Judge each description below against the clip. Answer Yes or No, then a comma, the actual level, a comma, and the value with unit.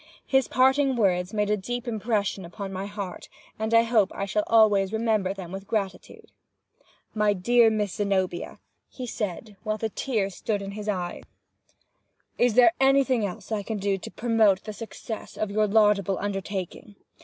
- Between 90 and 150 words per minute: No, average, 165 wpm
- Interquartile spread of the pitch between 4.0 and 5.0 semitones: No, narrow, 2.5 semitones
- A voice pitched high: Yes, high, 210 Hz